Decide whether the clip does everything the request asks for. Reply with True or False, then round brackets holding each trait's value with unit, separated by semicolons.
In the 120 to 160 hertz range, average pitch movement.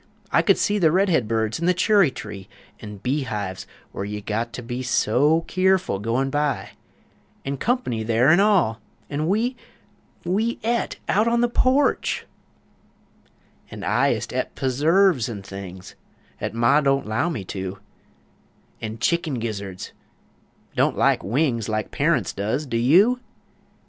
False (135 Hz; 8.4 semitones)